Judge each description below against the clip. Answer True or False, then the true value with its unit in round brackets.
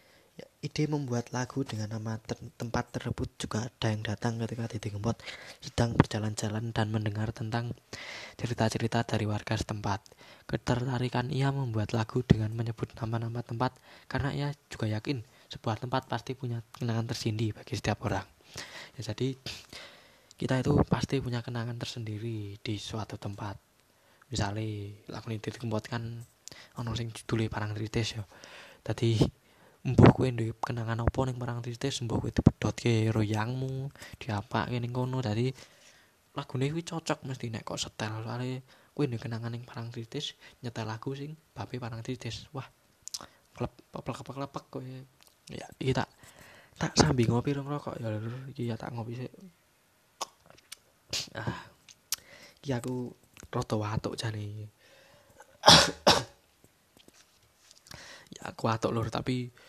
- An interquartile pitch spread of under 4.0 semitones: True (2.7 semitones)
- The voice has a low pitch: True (115 Hz)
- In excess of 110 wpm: True (135 wpm)